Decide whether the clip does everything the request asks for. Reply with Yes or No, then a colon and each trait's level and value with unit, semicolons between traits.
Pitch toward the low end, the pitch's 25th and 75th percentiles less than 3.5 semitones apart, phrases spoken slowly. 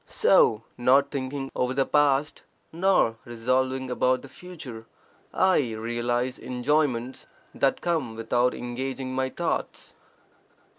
Yes: low, 130 Hz; narrow, 2.6 semitones; slow, 110 wpm